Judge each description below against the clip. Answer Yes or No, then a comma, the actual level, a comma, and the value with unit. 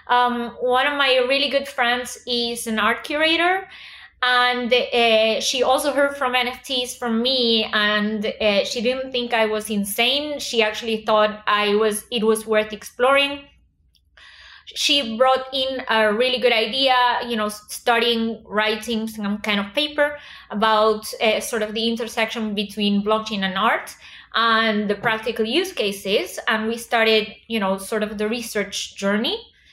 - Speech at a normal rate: Yes, average, 155 wpm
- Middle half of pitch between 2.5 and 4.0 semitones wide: Yes, average, 2.8 semitones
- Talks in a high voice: Yes, high, 230 Hz